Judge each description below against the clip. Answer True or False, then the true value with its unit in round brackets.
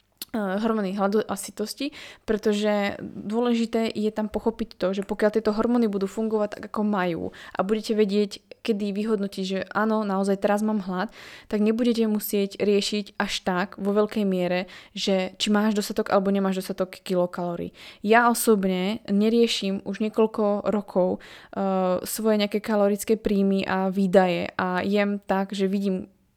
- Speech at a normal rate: True (150 wpm)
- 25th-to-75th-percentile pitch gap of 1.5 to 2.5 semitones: True (2.0 semitones)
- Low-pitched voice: False (205 Hz)